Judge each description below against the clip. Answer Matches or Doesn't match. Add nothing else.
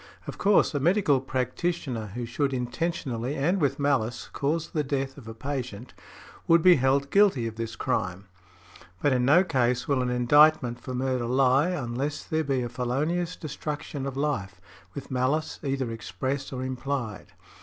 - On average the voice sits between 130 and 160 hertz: Matches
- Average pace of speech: Matches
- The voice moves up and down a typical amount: Matches